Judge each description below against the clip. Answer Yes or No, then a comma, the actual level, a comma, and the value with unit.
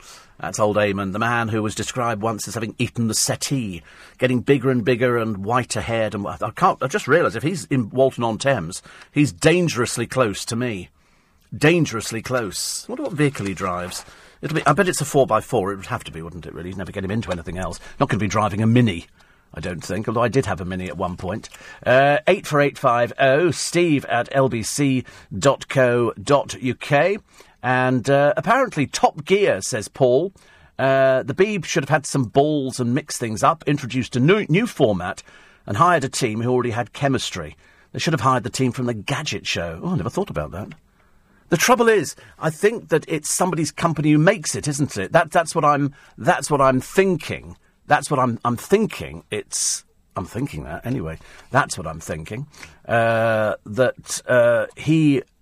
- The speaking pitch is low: Yes, low, 125 Hz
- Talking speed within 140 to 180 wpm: No, average, 195 wpm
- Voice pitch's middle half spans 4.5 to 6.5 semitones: Yes, average, 5.1 semitones